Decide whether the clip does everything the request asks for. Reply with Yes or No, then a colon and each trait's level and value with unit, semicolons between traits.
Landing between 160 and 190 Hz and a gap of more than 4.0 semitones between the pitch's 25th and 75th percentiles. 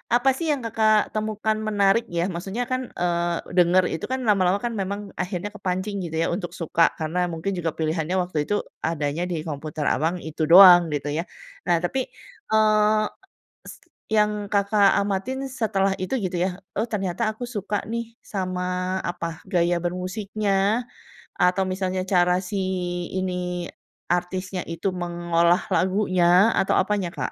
No: medium, 185 Hz; average, 3.1 semitones